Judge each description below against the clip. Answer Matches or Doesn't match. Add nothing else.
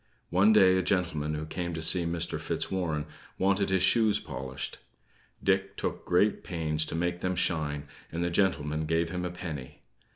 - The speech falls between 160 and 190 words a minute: Matches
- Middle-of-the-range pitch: Doesn't match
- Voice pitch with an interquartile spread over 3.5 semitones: Doesn't match